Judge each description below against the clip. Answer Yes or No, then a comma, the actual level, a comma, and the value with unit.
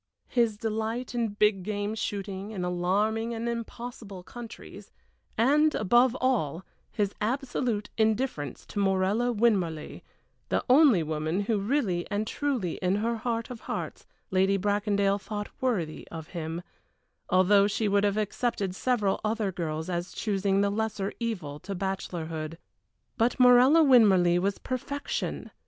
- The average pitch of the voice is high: Yes, high, 205 Hz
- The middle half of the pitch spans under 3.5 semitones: No, average, 3.9 semitones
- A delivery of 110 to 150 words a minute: Yes, slow, 135 wpm